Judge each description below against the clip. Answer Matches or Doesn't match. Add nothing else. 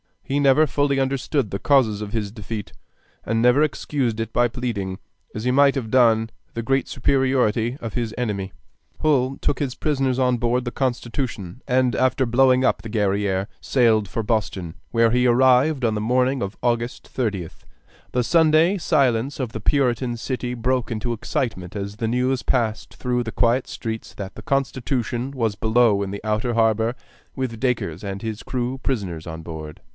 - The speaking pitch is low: Matches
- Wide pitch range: Doesn't match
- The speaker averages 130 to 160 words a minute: Doesn't match